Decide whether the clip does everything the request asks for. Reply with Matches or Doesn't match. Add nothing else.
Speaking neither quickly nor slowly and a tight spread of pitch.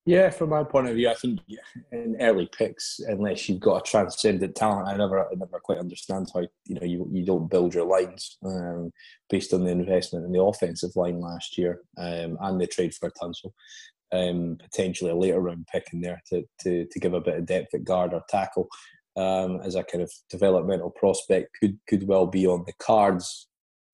Doesn't match